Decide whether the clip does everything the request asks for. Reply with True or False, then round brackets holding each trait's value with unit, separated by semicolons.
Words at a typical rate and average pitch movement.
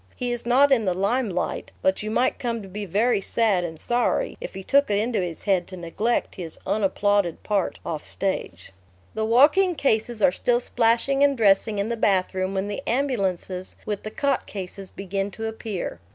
True (190 wpm; 4.0 semitones)